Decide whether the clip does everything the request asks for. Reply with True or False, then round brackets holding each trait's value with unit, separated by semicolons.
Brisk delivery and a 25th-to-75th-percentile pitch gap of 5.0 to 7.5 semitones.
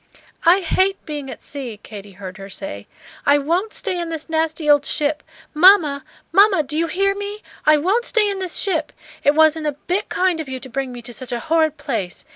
True (215 wpm; 5.4 semitones)